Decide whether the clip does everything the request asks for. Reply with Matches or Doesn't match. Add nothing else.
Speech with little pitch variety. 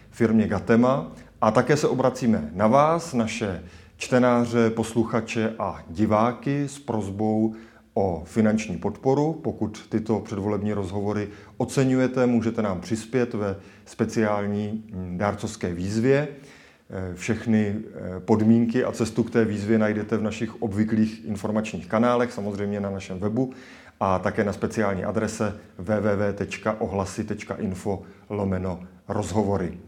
Matches